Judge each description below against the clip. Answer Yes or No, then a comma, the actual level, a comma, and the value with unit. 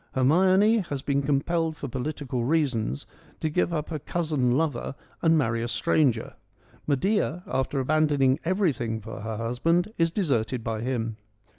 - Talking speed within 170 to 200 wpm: No, average, 150 wpm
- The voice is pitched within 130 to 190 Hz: Yes, medium, 140 Hz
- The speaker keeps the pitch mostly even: No, average, 5.1 semitones